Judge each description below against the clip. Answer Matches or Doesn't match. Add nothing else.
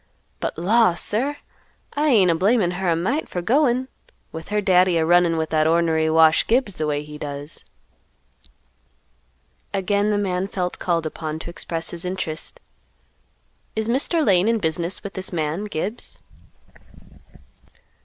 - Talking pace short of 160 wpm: Matches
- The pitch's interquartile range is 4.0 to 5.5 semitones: Matches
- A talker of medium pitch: Matches